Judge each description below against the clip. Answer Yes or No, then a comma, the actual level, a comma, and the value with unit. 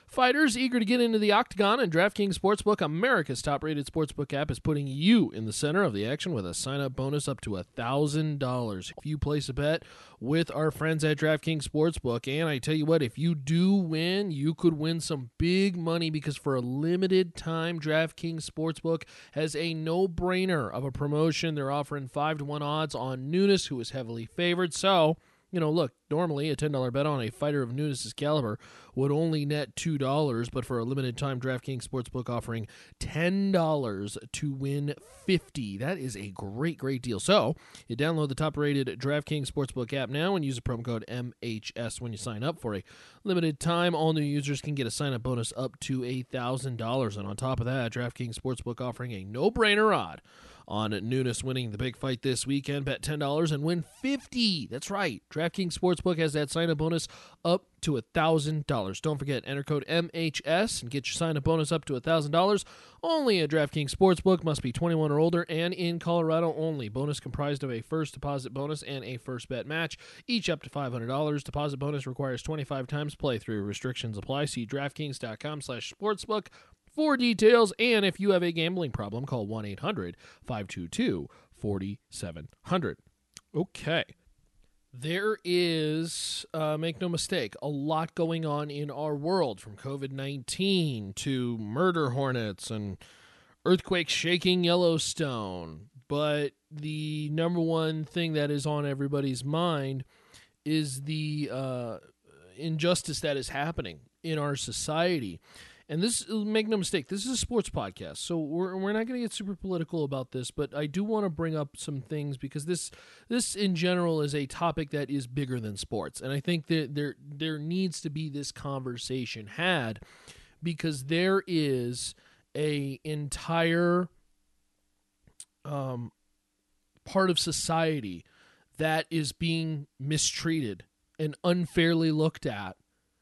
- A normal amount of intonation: Yes, average, 4.2 semitones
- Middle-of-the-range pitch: Yes, medium, 150 Hz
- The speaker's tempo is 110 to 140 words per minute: No, average, 170 wpm